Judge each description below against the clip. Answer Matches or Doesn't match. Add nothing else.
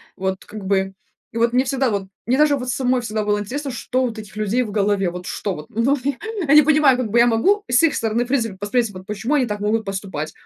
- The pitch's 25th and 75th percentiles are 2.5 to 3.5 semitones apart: Doesn't match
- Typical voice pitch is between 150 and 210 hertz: Doesn't match